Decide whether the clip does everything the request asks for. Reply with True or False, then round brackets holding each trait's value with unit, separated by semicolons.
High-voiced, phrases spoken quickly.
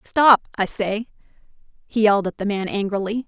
False (210 Hz; 165 wpm)